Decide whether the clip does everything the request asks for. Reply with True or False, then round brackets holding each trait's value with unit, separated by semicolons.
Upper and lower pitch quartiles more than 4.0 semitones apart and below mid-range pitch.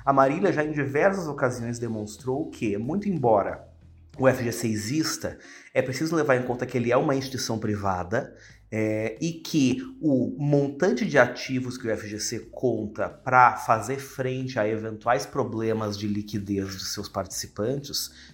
True (4.5 semitones; 120 Hz)